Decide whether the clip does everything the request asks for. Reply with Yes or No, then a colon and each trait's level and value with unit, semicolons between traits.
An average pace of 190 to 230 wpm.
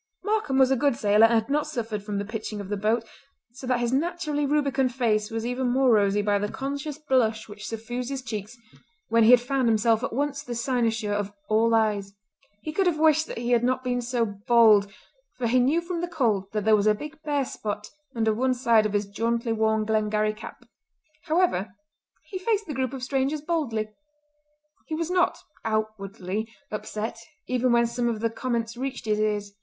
Yes: fast, 205 wpm